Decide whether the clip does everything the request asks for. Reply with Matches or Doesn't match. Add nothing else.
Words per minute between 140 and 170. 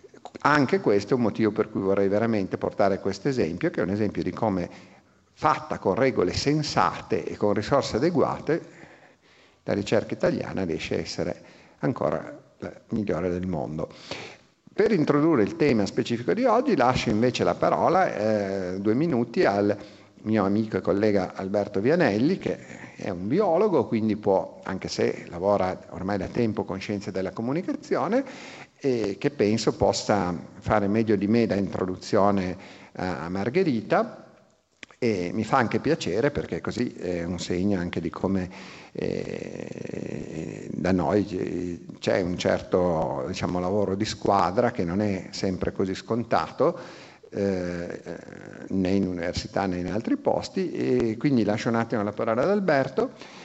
Matches